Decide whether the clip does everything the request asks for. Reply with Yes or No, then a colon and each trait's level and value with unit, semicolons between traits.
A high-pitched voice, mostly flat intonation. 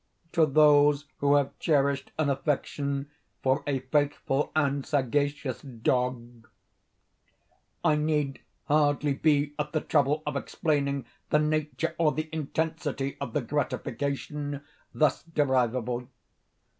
No: medium, 145 Hz; narrow, 1.8 semitones